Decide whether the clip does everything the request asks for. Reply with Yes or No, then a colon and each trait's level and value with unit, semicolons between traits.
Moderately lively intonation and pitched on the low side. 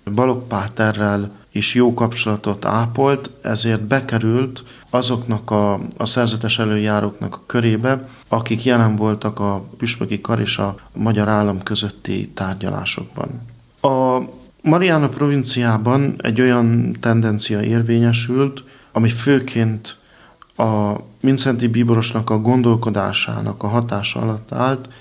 Yes: average, 3.0 semitones; low, 115 Hz